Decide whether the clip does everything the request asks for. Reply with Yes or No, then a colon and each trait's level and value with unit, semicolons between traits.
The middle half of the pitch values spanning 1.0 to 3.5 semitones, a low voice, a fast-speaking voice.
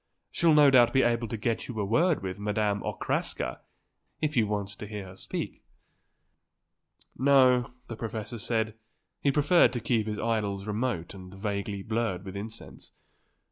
No: average, 3.2 semitones; low, 110 Hz; average, 160 wpm